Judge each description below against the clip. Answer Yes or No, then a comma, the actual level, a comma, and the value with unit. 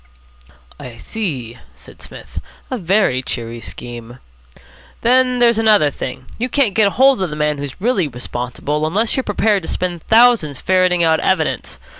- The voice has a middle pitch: Yes, medium, 180 Hz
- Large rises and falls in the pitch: Yes, wide, 8.6 semitones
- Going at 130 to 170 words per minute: Yes, average, 155 wpm